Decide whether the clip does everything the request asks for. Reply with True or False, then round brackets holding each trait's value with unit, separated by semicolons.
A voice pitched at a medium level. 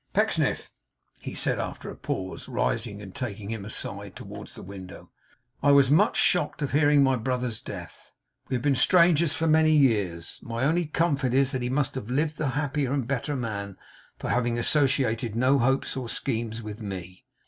False (130 Hz)